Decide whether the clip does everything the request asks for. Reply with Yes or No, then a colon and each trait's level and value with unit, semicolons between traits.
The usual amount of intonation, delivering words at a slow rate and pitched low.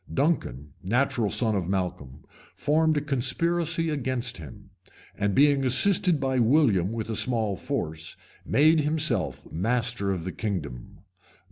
No: wide, 7.1 semitones; slow, 130 wpm; low, 120 Hz